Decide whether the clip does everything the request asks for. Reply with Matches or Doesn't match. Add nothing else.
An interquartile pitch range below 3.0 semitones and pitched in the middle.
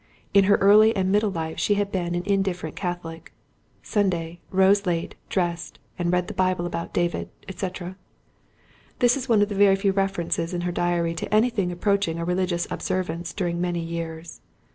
Matches